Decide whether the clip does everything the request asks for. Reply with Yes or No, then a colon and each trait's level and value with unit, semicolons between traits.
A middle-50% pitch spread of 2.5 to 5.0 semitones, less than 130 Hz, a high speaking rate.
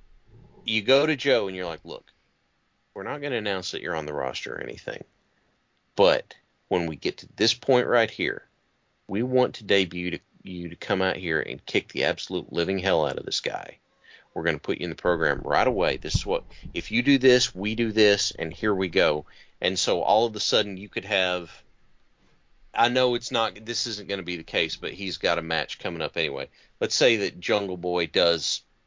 Yes: average, 4.7 semitones; low, 105 Hz; fast, 220 wpm